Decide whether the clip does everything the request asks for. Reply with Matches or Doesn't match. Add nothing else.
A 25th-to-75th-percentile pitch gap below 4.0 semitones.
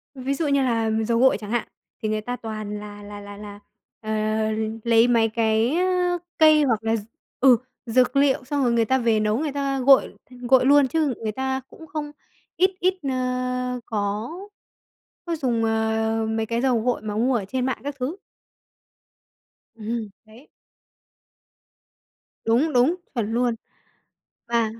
Matches